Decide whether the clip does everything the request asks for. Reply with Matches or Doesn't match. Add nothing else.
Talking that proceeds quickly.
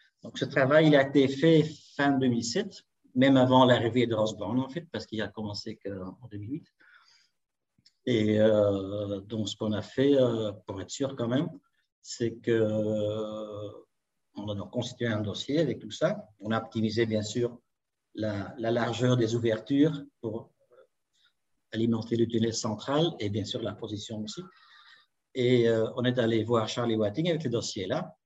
Doesn't match